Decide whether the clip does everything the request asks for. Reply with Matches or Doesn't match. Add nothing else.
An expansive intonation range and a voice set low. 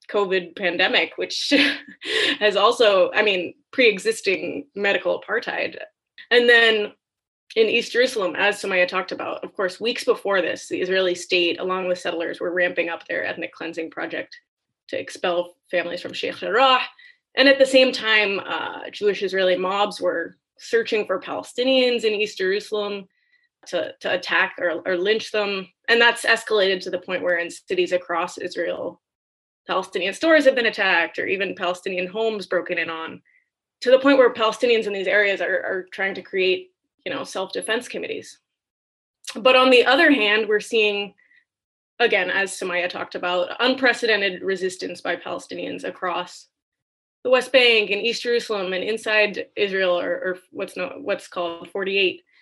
Doesn't match